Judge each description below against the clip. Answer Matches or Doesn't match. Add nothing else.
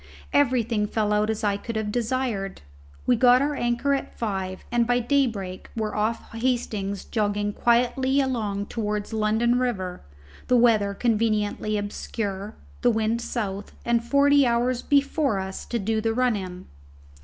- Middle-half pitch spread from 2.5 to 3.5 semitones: Matches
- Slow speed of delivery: Doesn't match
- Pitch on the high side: Matches